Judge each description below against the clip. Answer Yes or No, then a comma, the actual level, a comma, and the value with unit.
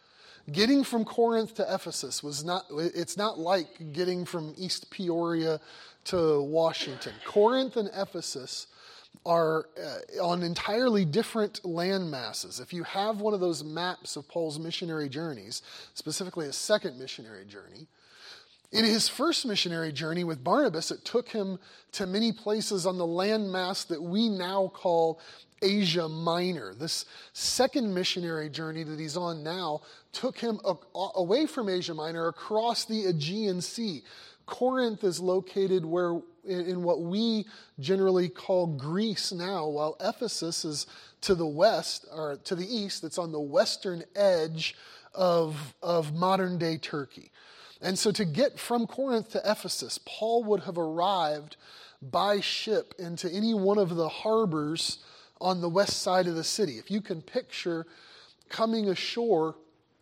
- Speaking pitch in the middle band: Yes, medium, 180 Hz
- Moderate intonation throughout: Yes, average, 4.2 semitones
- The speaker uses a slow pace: No, average, 150 wpm